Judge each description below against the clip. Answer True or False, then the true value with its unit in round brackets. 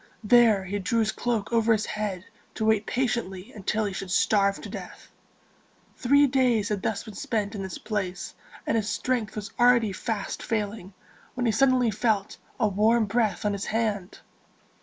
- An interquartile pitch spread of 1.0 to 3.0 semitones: True (2.6 semitones)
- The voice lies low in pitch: False (215 Hz)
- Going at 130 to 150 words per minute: False (175 wpm)